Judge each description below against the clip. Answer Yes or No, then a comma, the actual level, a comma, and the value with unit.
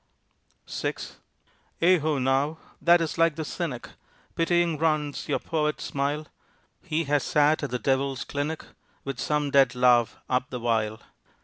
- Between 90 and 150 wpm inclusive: Yes, average, 145 wpm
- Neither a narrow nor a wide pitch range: Yes, average, 3.1 semitones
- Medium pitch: Yes, medium, 145 Hz